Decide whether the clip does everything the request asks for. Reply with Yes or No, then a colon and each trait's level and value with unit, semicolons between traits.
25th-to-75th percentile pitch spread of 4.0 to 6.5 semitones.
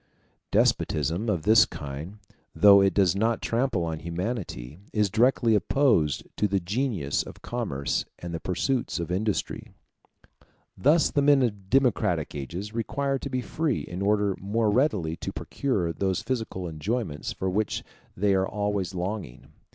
Yes: average, 5.0 semitones